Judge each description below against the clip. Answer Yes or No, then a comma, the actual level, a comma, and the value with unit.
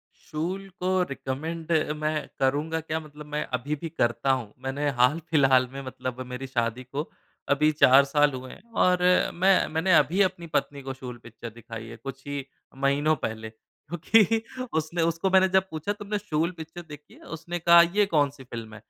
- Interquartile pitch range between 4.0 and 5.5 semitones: Yes, average, 4.4 semitones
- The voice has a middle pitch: Yes, medium, 150 Hz